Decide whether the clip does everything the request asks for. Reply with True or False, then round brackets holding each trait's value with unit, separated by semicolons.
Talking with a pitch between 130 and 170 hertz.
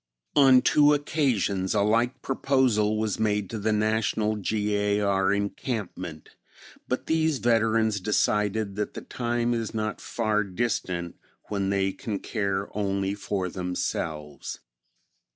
False (105 Hz)